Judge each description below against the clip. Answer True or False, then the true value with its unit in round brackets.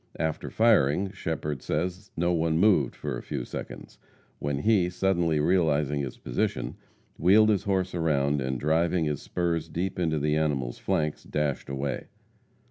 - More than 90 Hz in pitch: False (80 Hz)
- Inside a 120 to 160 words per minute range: True (150 wpm)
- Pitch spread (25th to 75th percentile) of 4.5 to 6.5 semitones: False (3.8 semitones)